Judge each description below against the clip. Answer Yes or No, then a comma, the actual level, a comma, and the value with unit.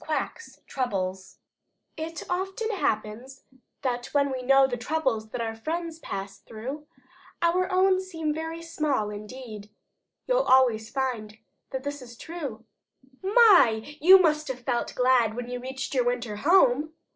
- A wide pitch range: Yes, wide, 5.8 semitones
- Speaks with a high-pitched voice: Yes, very high, 265 Hz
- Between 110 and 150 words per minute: Yes, average, 140 wpm